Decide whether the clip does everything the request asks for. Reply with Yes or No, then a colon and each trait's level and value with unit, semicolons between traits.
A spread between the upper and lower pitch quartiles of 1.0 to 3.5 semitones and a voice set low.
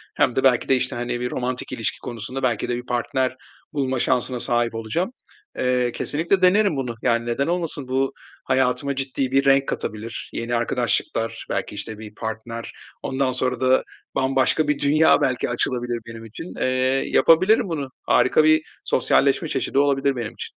Yes: narrow, 2.5 semitones; low, 130 Hz